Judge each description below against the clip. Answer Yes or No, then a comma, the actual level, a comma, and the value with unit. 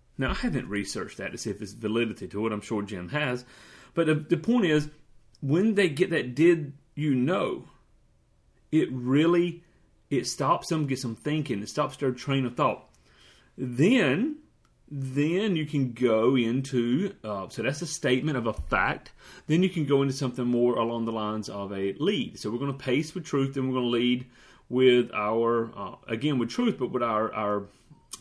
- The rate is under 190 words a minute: No, average, 195 wpm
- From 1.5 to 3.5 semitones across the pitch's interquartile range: No, average, 4.7 semitones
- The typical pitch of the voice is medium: No, low, 130 Hz